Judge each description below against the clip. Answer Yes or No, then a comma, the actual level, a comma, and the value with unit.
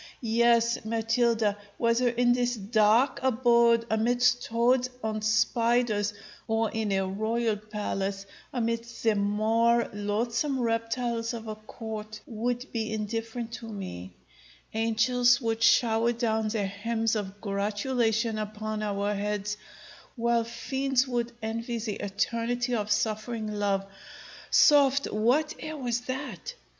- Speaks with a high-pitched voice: Yes, high, 225 Hz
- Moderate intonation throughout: No, narrow, 2.0 semitones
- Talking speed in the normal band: No, slow, 120 wpm